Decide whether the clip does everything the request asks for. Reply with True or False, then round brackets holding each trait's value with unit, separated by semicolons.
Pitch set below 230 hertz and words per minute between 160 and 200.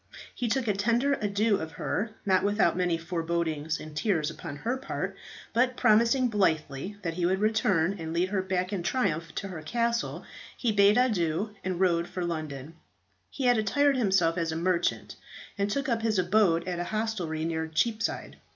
True (190 Hz; 180 wpm)